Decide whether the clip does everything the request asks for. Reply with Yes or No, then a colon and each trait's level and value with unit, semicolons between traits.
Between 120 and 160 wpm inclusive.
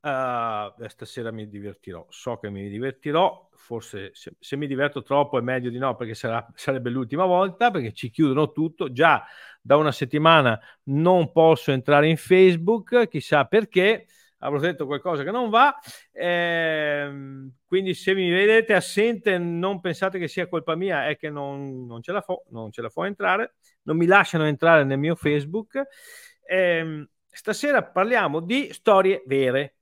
No: fast, 170 wpm